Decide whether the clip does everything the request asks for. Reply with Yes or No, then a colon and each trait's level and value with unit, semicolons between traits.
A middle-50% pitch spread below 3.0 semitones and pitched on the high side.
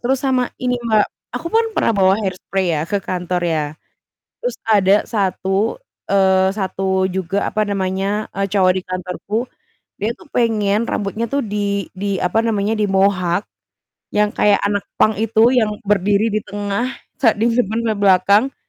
Yes: narrow, 2.5 semitones; high, 200 Hz